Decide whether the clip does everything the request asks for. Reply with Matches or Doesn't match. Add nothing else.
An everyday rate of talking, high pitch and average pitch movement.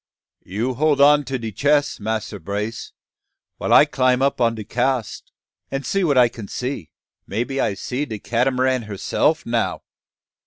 Doesn't match